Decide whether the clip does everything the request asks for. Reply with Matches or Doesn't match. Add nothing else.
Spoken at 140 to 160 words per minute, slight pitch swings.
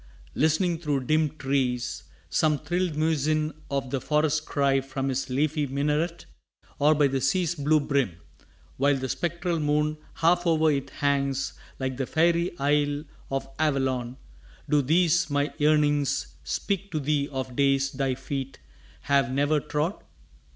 Matches